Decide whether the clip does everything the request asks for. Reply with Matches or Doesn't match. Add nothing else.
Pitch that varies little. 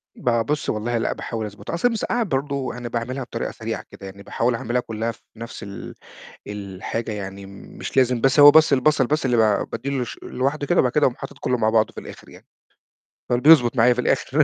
Doesn't match